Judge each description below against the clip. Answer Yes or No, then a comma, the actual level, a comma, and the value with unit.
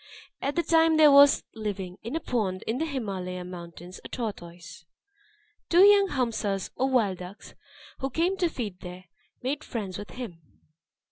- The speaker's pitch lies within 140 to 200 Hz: No, high, 220 Hz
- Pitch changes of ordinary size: No, wide, 7.6 semitones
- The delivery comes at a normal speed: Yes, average, 160 wpm